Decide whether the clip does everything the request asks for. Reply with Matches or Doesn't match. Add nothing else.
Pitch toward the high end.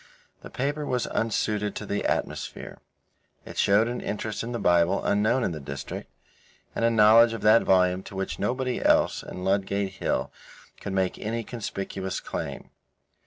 Doesn't match